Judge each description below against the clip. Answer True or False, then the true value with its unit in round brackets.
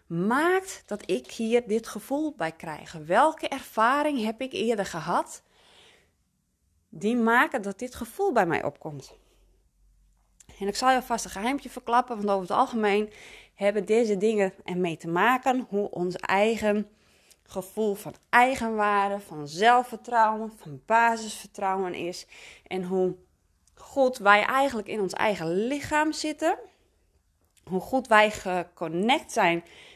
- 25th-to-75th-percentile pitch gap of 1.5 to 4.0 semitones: False (5.1 semitones)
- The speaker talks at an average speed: False (130 wpm)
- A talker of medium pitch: False (210 Hz)